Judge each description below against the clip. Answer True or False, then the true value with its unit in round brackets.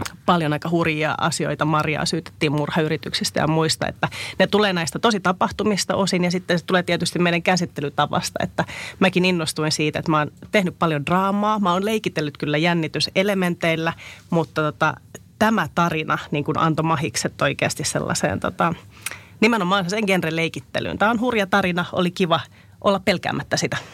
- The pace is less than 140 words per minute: False (155 wpm)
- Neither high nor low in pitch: True (170 Hz)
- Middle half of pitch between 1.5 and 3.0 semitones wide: False (3.5 semitones)